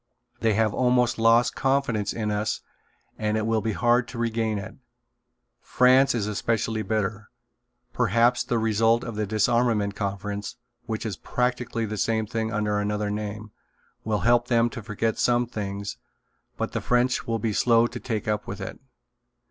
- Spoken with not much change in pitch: Yes, narrow, 2.1 semitones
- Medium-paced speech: Yes, average, 165 wpm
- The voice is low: Yes, low, 110 Hz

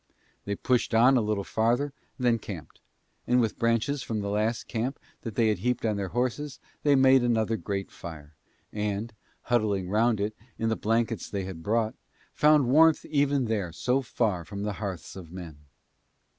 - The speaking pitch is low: Yes, low, 110 Hz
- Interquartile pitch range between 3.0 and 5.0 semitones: Yes, average, 3.6 semitones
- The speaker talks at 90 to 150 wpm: No, average, 185 wpm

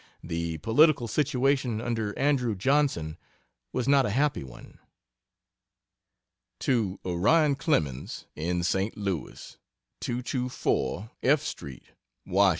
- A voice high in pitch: No, low, 115 Hz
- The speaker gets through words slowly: Yes, slow, 100 wpm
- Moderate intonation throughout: No, wide, 7.3 semitones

